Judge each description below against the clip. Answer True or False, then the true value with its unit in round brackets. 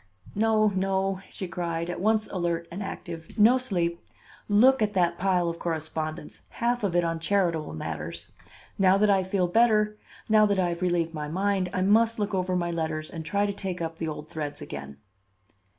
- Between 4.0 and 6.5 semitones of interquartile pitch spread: False (3.5 semitones)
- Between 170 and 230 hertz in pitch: True (185 Hz)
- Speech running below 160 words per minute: False (190 wpm)